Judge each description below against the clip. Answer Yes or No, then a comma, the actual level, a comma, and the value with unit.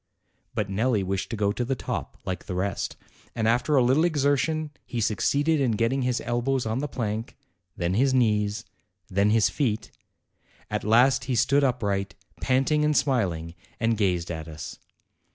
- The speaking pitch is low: Yes, low, 115 Hz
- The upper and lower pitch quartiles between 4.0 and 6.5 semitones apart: Yes, average, 4.7 semitones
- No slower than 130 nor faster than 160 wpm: No, average, 170 wpm